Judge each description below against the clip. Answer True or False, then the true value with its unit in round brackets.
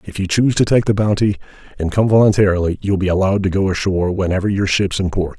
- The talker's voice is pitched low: True (95 Hz)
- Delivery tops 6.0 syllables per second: True (6.8 syllables/s)